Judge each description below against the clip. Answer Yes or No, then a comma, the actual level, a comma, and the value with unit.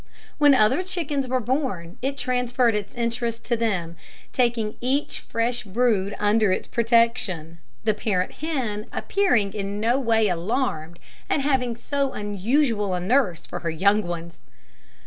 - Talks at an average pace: Yes, average, 145 wpm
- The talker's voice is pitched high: Yes, high, 230 Hz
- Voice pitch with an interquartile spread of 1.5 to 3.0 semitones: No, average, 4.2 semitones